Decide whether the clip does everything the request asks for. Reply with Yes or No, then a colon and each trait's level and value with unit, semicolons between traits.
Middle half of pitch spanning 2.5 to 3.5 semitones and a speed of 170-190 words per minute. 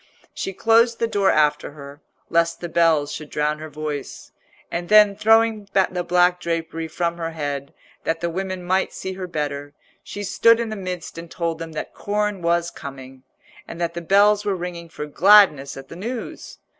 No: average, 4.3 semitones; average, 185 wpm